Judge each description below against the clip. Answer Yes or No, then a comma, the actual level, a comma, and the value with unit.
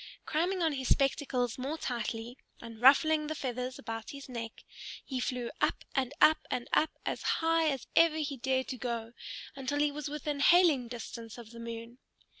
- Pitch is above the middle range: Yes, very high, 260 Hz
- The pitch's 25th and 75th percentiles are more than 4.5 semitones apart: No, average, 4.1 semitones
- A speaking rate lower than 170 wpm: No, average, 180 wpm